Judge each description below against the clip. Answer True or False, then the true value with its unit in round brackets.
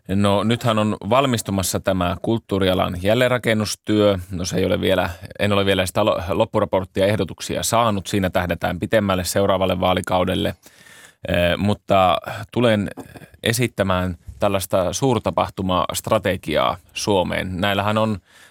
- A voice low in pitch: True (100 Hz)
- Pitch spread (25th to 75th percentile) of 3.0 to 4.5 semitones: False (2.6 semitones)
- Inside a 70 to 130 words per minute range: True (105 wpm)